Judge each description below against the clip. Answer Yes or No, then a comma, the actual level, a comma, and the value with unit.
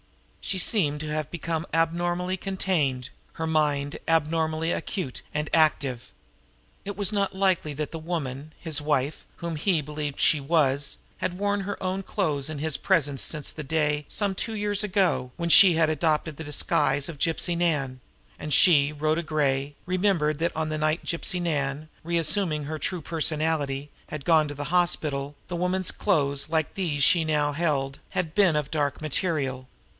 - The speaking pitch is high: No, medium, 155 Hz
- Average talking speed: Yes, average, 170 wpm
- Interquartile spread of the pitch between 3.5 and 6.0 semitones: No, average, 3.0 semitones